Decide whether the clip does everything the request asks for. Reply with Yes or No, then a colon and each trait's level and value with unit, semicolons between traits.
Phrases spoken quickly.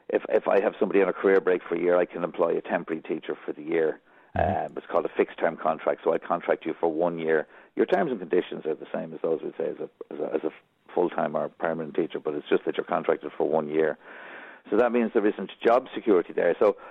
Yes: fast, 260 wpm